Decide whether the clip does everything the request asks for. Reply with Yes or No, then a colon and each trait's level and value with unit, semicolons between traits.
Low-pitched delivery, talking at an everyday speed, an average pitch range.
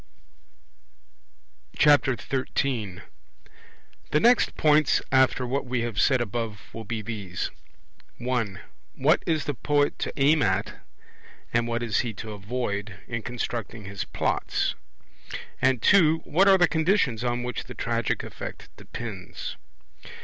No: low, 120 Hz; slow, 130 wpm; average, 4.6 semitones